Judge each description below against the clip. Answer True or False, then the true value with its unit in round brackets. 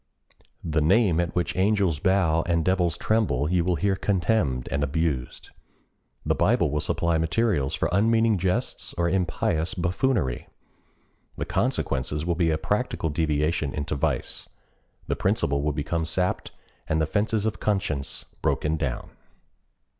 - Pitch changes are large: False (4.2 semitones)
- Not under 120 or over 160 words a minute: True (140 wpm)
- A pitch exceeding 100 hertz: False (85 Hz)